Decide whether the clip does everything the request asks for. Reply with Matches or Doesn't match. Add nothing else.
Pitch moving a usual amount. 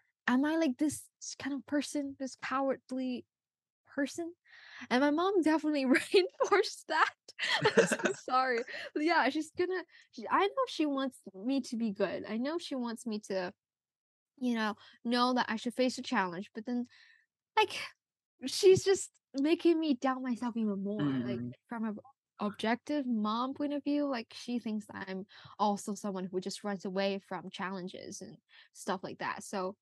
Doesn't match